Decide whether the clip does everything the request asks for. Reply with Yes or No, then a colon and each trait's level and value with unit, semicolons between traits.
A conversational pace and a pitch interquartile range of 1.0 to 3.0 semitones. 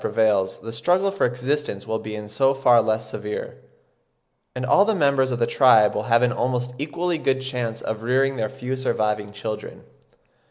No: average, 185 wpm; average, 3.5 semitones